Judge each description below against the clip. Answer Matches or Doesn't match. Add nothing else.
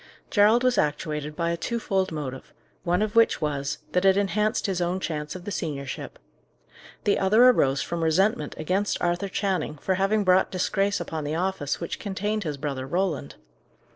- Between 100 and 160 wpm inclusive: Doesn't match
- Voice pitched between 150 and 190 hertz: Matches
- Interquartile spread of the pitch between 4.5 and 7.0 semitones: Matches